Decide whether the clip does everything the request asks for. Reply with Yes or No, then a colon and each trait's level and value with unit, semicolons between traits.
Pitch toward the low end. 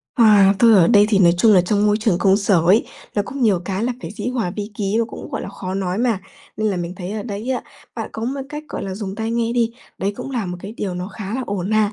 No: high, 205 Hz